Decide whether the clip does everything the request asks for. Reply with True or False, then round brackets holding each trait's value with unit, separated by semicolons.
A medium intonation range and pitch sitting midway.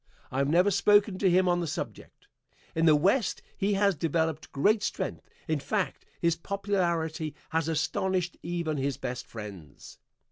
True (3.7 semitones; 170 Hz)